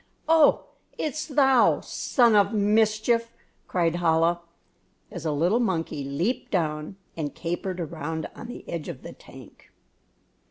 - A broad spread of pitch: Yes, wide, 6.0 semitones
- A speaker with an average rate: No, slow, 130 wpm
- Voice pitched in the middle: Yes, medium, 180 Hz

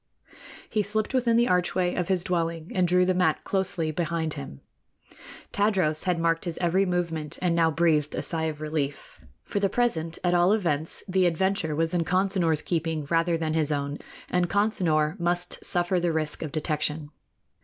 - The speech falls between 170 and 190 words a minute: Yes, average, 175 wpm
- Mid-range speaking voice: Yes, medium, 170 Hz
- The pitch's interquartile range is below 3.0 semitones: Yes, narrow, 2.6 semitones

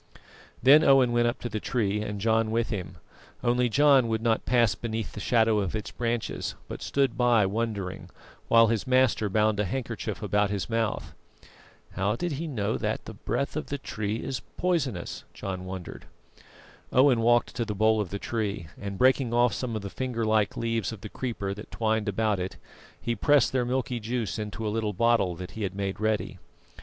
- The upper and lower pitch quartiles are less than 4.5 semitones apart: Yes, average, 2.8 semitones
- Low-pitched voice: Yes, low, 110 Hz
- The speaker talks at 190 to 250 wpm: Yes, average, 195 wpm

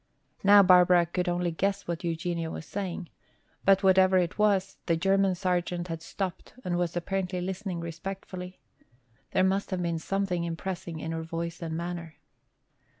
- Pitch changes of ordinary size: No, narrow, 2.1 semitones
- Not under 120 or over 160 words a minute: Yes, average, 155 wpm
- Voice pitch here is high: No, medium, 180 Hz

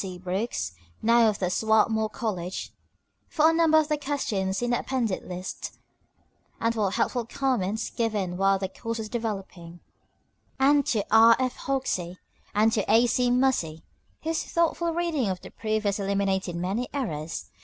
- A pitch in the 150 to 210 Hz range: No, high, 220 Hz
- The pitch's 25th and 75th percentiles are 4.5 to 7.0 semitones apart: Yes, average, 5.0 semitones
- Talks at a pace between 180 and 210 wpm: No, average, 155 wpm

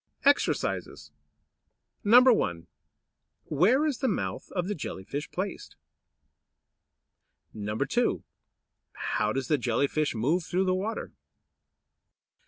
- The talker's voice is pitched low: No, medium, 175 Hz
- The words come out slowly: Yes, slow, 100 wpm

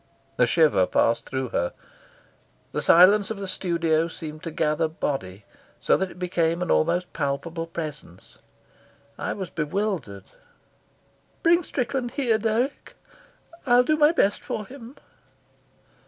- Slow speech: Yes, slow, 130 wpm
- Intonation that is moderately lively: No, wide, 6.2 semitones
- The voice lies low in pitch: No, medium, 170 Hz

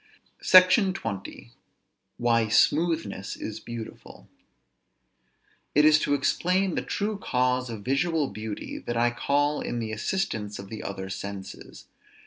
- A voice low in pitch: Yes, low, 125 Hz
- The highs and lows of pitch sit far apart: Yes, wide, 6.8 semitones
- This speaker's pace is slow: Yes, slow, 125 wpm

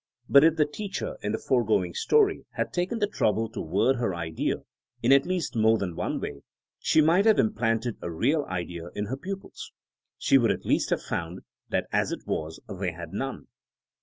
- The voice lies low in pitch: Yes, low, 115 Hz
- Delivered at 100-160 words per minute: No, average, 195 wpm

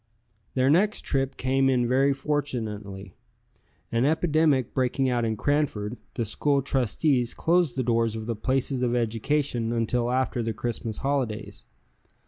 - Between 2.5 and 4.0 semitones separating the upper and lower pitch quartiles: Yes, average, 3.2 semitones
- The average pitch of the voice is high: No, low, 125 Hz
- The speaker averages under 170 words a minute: Yes, average, 140 wpm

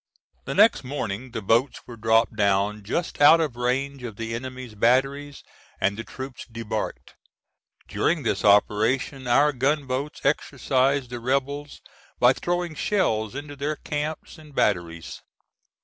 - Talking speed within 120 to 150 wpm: Yes, average, 140 wpm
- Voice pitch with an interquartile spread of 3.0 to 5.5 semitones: Yes, average, 4.1 semitones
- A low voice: Yes, low, 130 Hz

